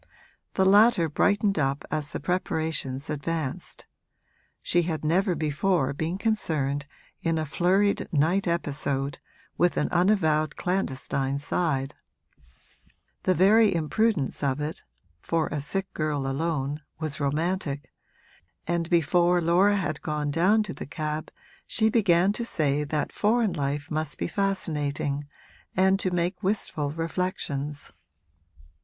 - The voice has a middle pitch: Yes, medium, 165 Hz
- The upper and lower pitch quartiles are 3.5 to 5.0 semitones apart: Yes, average, 4.3 semitones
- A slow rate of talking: Yes, slow, 125 wpm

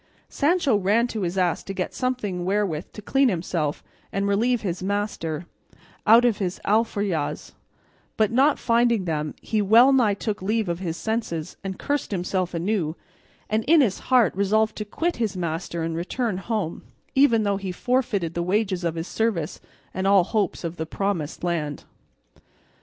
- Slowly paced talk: No, average, 170 wpm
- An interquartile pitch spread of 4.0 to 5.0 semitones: Yes, average, 4.5 semitones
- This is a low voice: No, high, 200 Hz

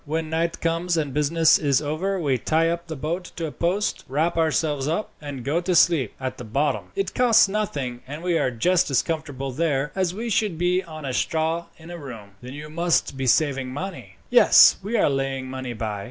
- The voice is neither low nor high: Yes, medium, 155 Hz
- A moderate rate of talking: No, fast, 210 wpm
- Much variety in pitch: No, average, 4.0 semitones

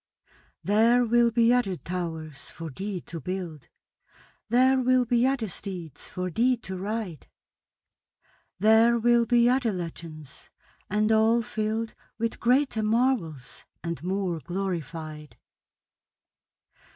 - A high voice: Yes, high, 215 Hz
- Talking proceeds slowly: Yes, slow, 115 wpm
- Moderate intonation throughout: No, wide, 5.7 semitones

